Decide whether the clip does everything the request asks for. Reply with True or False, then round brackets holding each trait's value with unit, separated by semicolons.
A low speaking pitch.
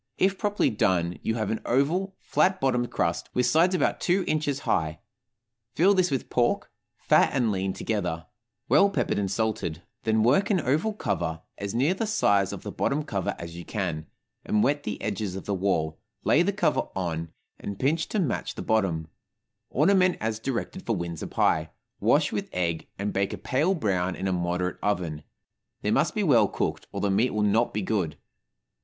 True (110 Hz)